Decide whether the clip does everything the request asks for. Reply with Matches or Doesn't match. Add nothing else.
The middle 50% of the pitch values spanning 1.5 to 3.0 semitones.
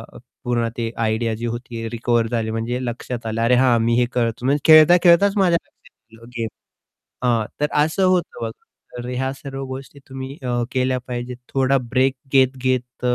Matches